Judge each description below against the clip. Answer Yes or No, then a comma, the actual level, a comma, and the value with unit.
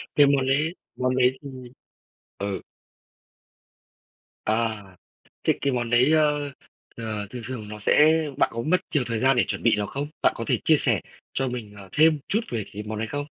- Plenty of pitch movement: No, average, 4.7 semitones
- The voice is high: No, low, 125 Hz